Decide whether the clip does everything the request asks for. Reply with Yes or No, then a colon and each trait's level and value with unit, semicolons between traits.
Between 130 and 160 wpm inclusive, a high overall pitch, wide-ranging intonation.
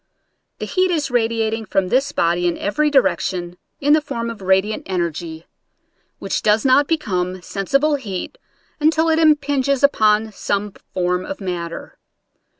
Yes: average, 150 wpm; high, 220 Hz; wide, 7.6 semitones